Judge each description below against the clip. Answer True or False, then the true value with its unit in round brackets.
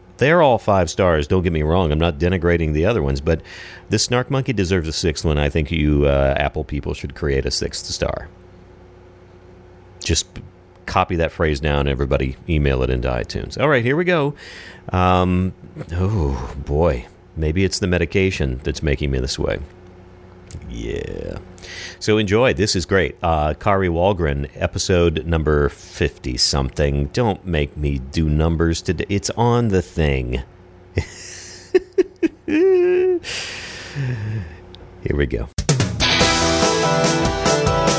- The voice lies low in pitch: True (90 Hz)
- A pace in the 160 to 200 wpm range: False (135 wpm)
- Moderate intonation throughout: True (3.7 semitones)